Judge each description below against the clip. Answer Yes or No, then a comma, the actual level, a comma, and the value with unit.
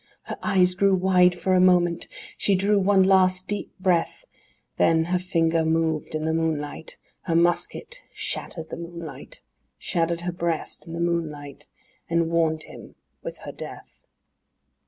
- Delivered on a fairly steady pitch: Yes, narrow, 2.1 semitones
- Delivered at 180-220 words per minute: No, average, 145 wpm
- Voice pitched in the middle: Yes, medium, 170 Hz